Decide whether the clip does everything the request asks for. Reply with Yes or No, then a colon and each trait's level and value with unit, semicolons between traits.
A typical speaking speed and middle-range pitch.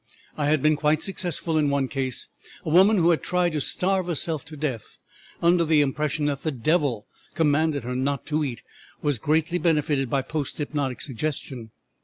Yes: average, 180 wpm; medium, 150 Hz